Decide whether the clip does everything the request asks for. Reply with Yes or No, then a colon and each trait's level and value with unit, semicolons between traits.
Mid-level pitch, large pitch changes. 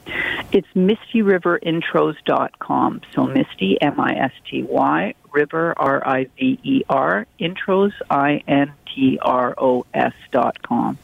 Yes: medium, 165 Hz; wide, 6.3 semitones